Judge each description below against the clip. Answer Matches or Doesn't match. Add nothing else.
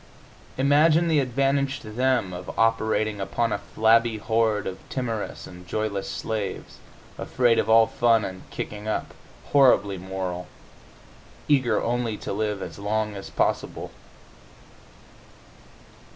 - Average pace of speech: Doesn't match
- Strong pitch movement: Doesn't match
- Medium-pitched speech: Doesn't match